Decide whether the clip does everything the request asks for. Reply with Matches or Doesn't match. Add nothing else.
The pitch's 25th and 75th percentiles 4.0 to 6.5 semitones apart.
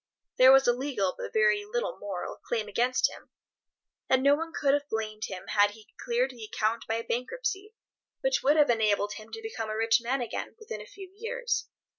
Matches